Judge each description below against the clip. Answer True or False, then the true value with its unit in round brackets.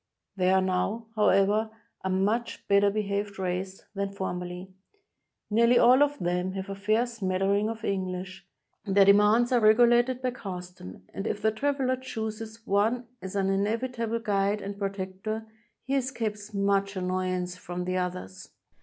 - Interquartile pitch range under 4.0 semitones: True (3.0 semitones)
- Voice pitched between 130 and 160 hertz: False (200 Hz)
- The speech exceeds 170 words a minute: False (145 wpm)